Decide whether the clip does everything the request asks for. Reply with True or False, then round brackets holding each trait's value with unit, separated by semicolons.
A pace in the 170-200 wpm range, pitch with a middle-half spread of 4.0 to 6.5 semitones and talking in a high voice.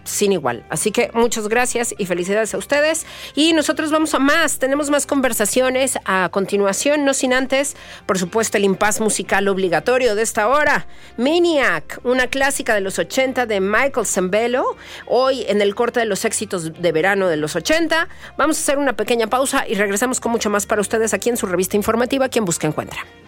True (190 wpm; 5.1 semitones; 230 Hz)